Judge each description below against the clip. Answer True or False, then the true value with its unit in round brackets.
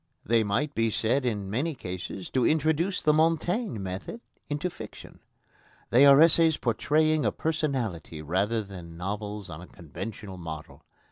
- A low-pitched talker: True (115 Hz)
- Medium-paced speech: True (145 wpm)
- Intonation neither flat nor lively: False (8.1 semitones)